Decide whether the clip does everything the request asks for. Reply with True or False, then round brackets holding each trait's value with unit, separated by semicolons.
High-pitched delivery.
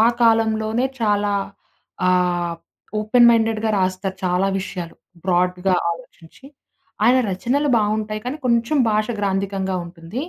True (205 Hz)